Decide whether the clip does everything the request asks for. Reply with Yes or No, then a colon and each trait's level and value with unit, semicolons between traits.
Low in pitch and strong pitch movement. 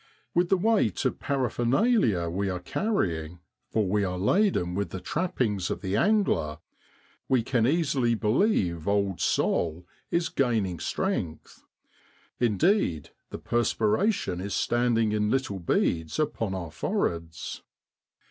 Yes: low, 105 Hz; wide, 7.1 semitones